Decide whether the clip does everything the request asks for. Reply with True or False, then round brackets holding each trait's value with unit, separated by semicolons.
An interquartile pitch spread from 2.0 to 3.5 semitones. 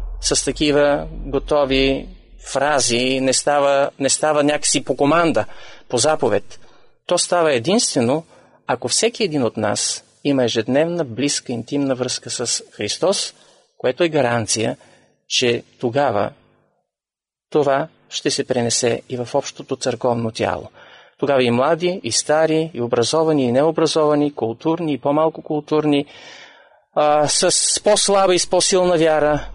False (4.1 semitones)